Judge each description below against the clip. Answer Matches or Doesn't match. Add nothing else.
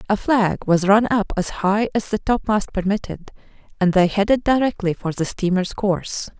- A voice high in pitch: Matches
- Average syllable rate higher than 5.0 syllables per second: Doesn't match